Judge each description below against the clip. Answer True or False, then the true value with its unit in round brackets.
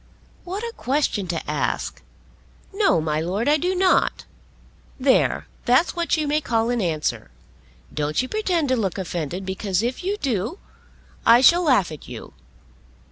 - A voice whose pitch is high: True (245 Hz)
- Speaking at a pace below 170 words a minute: True (155 wpm)